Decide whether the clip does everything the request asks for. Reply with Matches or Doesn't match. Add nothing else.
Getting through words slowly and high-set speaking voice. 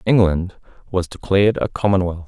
Doesn't match